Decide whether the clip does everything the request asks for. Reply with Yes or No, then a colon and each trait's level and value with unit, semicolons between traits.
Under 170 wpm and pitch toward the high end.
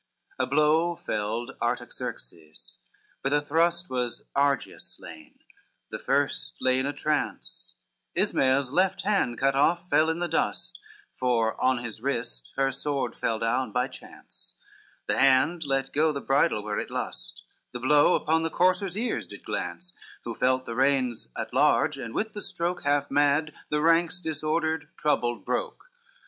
No: average, 160 wpm; medium, 140 Hz